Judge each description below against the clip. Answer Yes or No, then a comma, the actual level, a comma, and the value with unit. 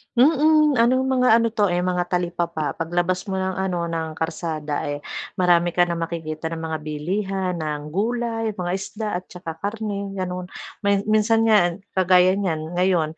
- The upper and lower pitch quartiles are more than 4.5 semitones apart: No, average, 3.7 semitones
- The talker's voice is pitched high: No, medium, 180 Hz